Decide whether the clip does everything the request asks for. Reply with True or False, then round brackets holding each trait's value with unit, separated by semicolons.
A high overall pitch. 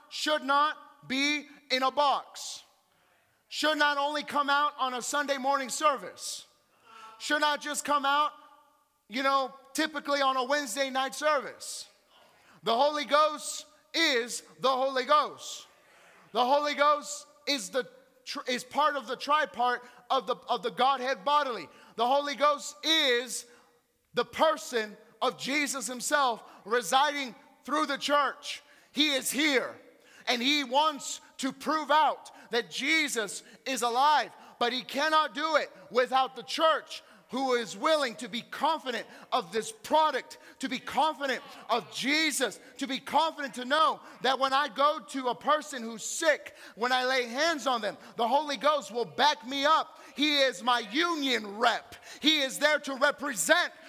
True (280 Hz)